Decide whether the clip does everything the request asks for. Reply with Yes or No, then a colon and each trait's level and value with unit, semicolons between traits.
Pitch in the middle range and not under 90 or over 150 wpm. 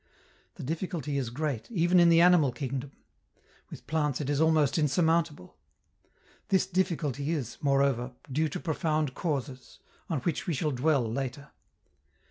Yes: medium, 150 Hz; average, 140 wpm